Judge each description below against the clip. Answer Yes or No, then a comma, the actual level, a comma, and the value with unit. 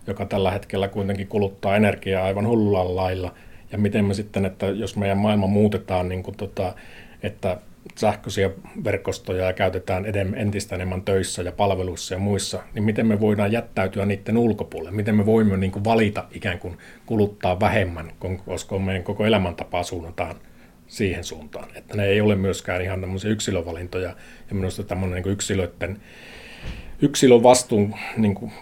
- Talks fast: Yes, fast, 160 wpm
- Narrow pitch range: Yes, narrow, 2.3 semitones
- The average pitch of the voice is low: Yes, low, 100 Hz